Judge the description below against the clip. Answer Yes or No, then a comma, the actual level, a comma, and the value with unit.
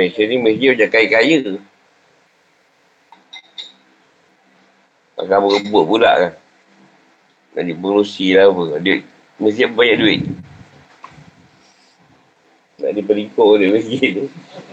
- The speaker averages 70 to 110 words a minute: Yes, average, 100 wpm